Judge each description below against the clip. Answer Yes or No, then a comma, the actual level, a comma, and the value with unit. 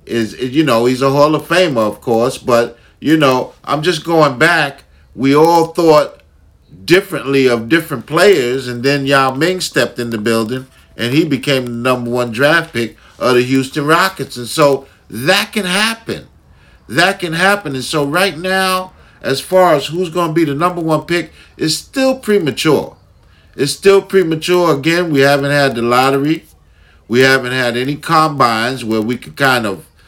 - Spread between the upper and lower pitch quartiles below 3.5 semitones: No, average, 5.3 semitones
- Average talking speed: Yes, average, 180 wpm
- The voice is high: No, medium, 140 Hz